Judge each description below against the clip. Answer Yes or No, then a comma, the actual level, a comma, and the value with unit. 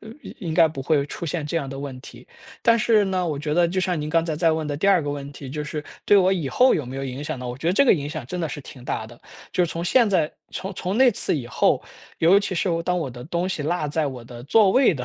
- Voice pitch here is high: No, medium, 160 Hz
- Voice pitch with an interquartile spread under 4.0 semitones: No, average, 4.6 semitones